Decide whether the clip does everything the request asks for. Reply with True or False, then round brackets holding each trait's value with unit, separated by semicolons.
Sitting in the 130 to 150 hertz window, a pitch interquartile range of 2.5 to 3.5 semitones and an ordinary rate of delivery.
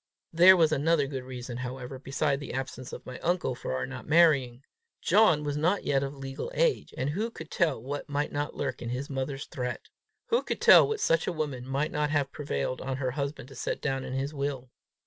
False (140 Hz; 2.8 semitones; 220 wpm)